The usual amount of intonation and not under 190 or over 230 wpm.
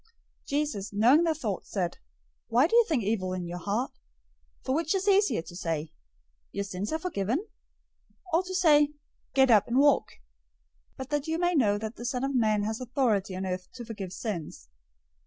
No: wide, 6.9 semitones; average, 195 wpm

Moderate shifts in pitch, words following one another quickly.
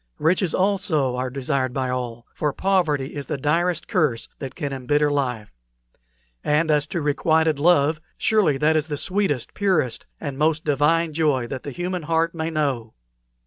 No: average, 3.5 semitones; average, 165 wpm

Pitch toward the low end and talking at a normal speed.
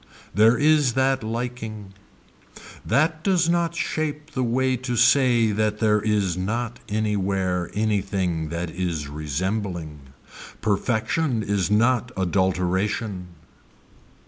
No: low, 110 Hz; slow, 105 wpm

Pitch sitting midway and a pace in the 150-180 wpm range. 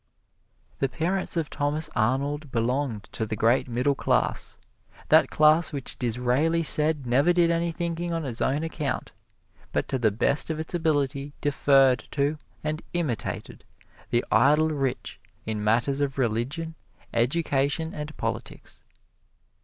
No: medium, 145 Hz; average, 140 wpm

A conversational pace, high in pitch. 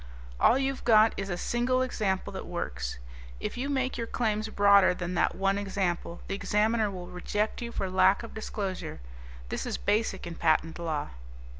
Yes: average, 175 wpm; high, 200 Hz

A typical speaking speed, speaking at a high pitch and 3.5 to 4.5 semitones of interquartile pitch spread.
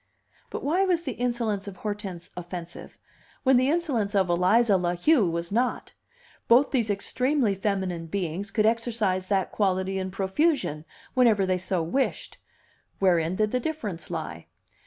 No: average, 150 wpm; high, 200 Hz; average, 5.0 semitones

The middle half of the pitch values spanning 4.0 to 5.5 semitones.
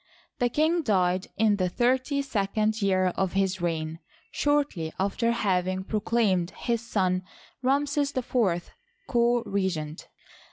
Yes: average, 4.7 semitones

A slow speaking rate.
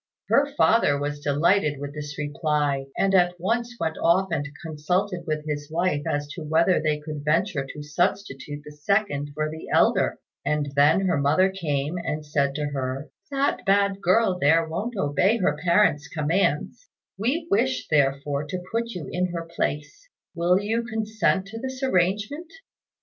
No: average, 165 wpm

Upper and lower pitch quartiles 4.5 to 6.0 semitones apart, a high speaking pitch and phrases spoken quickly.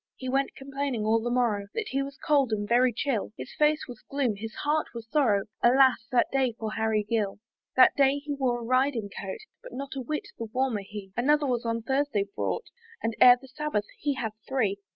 No: average, 3.7 semitones; very high, 250 Hz; fast, 215 wpm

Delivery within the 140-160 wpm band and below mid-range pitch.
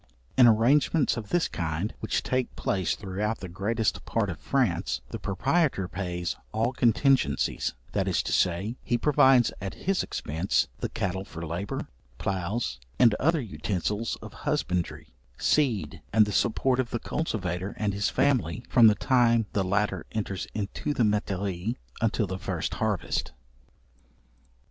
Yes: average, 150 wpm; low, 105 Hz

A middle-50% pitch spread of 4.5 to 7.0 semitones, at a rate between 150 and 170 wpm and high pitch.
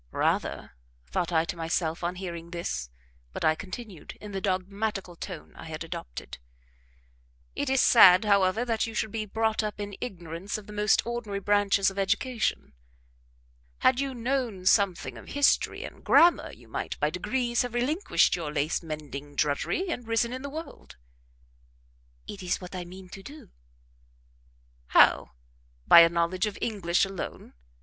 Yes: average, 5.0 semitones; average, 160 wpm; high, 195 Hz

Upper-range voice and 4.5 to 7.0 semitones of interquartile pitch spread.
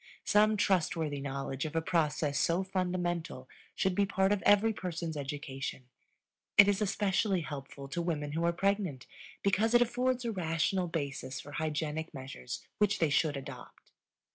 No: medium, 170 Hz; average, 5.1 semitones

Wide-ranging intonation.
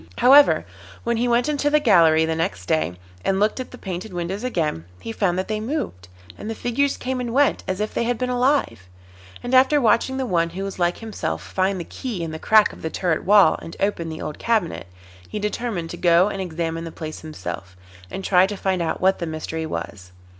Yes: wide, 6.4 semitones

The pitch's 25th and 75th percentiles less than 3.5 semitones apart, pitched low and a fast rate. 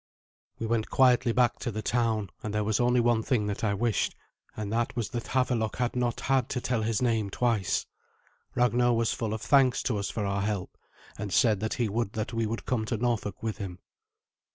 Yes: narrow, 2.4 semitones; low, 115 Hz; fast, 215 wpm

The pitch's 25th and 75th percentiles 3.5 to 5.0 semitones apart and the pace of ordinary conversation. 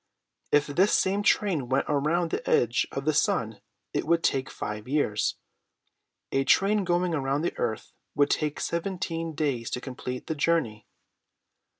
Yes: average, 4.5 semitones; average, 155 wpm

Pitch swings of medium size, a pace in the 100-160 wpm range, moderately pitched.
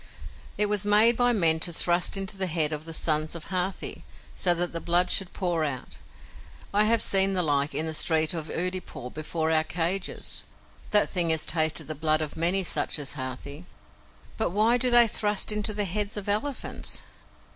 No: average, 4.4 semitones; average, 190 wpm; medium, 175 Hz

